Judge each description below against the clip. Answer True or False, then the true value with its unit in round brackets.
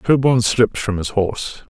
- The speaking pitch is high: False (110 Hz)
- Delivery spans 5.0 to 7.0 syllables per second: True (5.8 syllables/s)